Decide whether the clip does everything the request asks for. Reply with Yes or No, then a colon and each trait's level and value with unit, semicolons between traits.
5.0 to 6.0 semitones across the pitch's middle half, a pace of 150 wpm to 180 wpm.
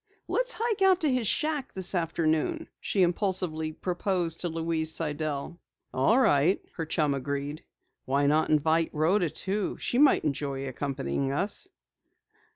No: average, 5.3 semitones; average, 140 wpm